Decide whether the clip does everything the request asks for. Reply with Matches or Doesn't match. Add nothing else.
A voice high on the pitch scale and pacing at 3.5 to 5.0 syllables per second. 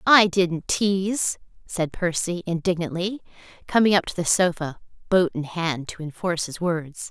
Doesn't match